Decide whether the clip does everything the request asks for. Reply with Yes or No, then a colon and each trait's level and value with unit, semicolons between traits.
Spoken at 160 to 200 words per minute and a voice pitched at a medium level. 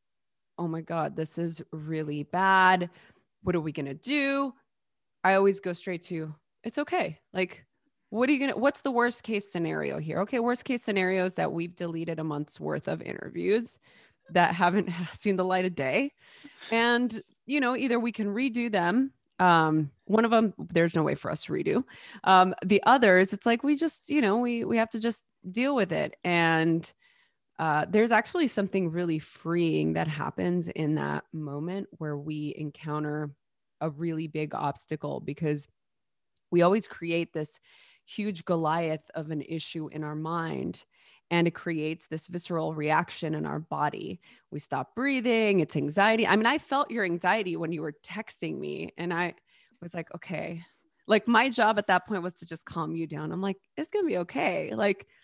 Yes: average, 180 wpm; medium, 180 Hz